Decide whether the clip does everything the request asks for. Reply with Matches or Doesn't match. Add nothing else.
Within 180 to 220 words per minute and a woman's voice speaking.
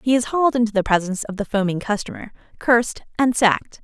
Matches